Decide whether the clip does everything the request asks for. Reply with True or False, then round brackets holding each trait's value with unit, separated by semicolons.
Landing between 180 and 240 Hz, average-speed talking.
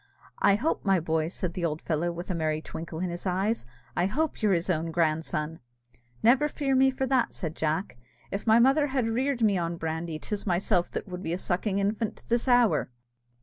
False (185 Hz; 215 wpm)